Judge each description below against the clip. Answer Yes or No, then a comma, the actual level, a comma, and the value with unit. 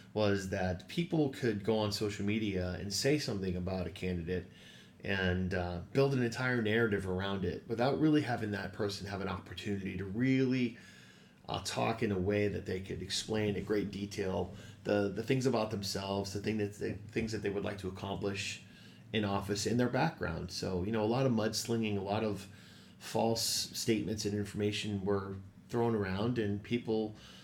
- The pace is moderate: Yes, average, 185 wpm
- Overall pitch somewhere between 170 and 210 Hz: No, low, 105 Hz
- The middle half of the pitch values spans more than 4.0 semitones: No, narrow, 2.4 semitones